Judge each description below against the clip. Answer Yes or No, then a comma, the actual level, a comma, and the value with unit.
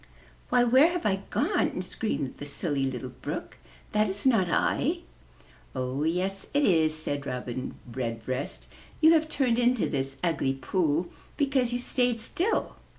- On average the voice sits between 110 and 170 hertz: No, medium, 180 Hz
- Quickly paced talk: No, average, 150 wpm